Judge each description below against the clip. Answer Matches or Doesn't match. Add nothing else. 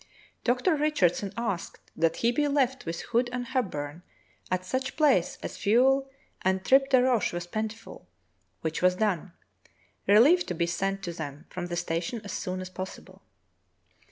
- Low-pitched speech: Doesn't match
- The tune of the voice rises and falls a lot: Matches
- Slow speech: Doesn't match